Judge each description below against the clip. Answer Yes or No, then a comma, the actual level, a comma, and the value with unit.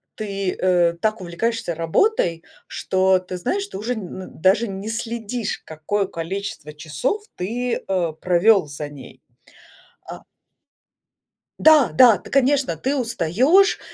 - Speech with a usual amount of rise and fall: No, wide, 5.7 semitones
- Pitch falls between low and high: No, high, 195 Hz